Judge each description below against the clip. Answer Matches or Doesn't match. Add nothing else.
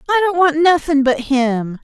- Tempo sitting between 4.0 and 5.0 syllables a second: Matches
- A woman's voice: Matches